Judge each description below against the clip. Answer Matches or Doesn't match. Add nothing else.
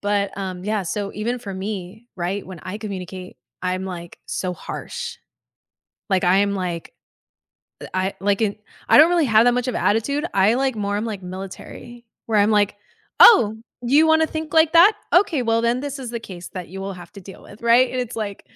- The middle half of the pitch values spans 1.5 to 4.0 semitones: Doesn't match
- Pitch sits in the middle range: Doesn't match